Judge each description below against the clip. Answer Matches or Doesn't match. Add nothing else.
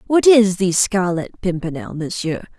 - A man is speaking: Doesn't match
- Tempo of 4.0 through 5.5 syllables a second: Matches